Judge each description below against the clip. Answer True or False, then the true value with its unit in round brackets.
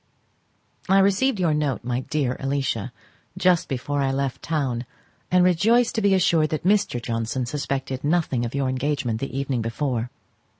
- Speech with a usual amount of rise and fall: False (5.7 semitones)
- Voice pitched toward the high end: False (140 Hz)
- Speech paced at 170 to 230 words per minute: False (160 wpm)